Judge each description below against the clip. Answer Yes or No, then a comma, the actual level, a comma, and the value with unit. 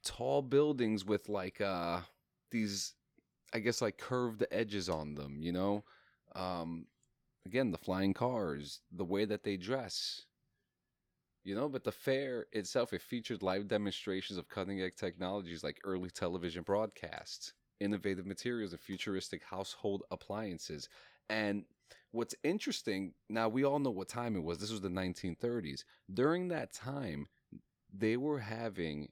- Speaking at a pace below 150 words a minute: Yes, average, 140 wpm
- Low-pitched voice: Yes, low, 100 Hz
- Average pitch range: Yes, average, 3.9 semitones